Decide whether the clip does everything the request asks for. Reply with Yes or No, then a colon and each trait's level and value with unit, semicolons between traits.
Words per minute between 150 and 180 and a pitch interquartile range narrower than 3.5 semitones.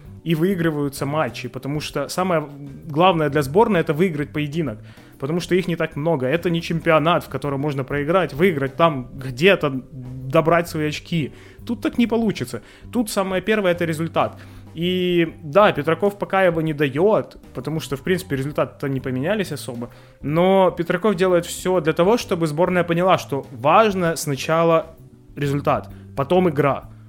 No: fast, 155 wpm; average, 4.7 semitones